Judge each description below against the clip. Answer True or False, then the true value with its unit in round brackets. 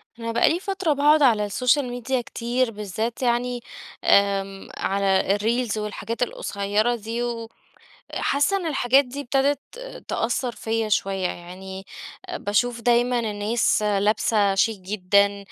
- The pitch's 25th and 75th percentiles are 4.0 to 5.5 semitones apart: False (3.6 semitones)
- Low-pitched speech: False (230 Hz)